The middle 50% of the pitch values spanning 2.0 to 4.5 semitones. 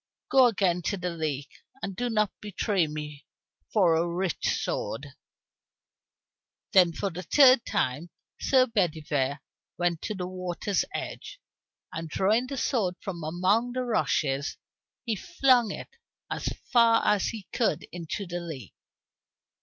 No: wide, 5.6 semitones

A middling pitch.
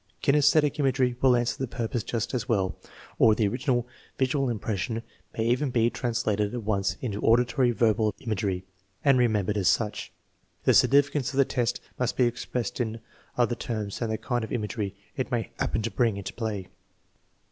No: low, 120 Hz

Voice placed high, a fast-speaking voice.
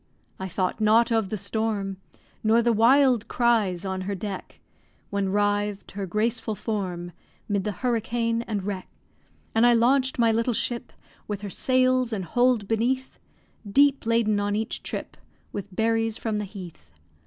No: high, 220 Hz; average, 155 wpm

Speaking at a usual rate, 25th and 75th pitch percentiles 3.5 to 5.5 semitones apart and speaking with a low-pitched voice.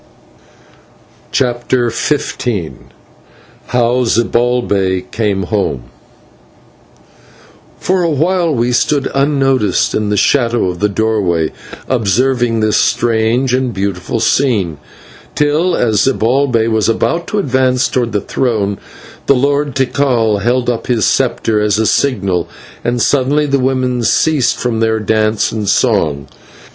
No: slow, 120 wpm; average, 3.8 semitones; low, 120 Hz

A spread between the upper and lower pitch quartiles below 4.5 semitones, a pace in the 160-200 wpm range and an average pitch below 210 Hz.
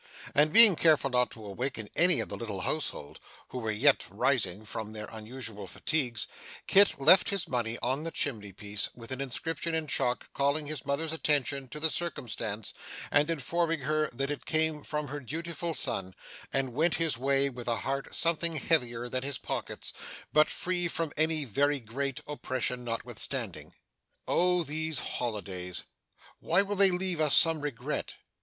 No: average, 5.0 semitones; average, 165 wpm; medium, 140 Hz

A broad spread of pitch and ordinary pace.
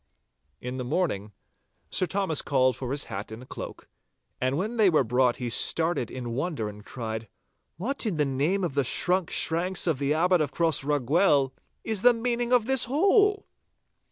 Yes: wide, 7.0 semitones; average, 175 wpm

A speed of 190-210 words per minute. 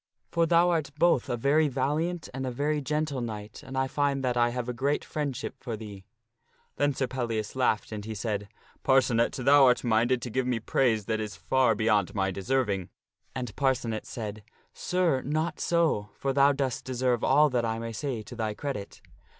Yes: average, 200 wpm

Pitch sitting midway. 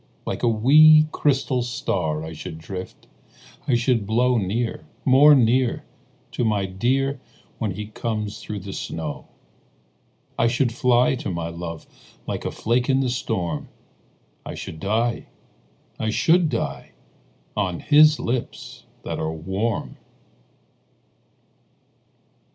No: low, 115 Hz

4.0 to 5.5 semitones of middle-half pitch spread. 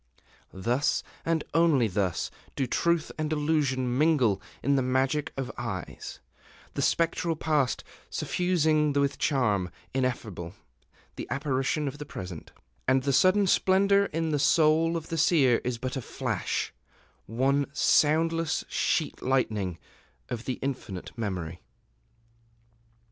Yes: average, 4.5 semitones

